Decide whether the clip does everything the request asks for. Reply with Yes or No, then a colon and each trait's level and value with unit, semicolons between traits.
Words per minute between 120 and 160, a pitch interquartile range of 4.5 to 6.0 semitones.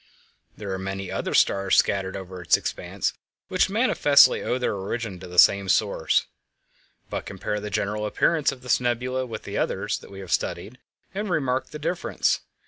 No: average, 175 wpm; average, 5.3 semitones